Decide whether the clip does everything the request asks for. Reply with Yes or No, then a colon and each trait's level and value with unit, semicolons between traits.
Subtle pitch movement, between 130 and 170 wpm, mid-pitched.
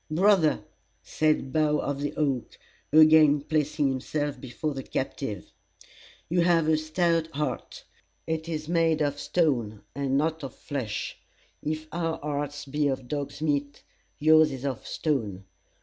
Yes: narrow, 2.2 semitones; average, 140 wpm; medium, 150 Hz